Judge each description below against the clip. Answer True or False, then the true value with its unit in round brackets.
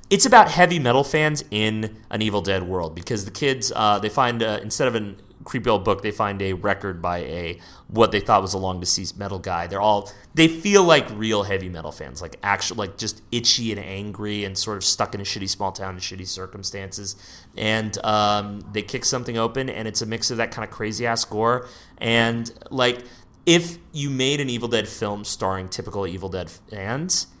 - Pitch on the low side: True (105 Hz)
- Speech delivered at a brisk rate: True (210 wpm)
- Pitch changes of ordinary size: True (3.3 semitones)